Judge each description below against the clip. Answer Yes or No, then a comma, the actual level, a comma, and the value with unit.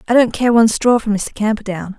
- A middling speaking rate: No, fast, 240 wpm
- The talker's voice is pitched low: No, high, 220 Hz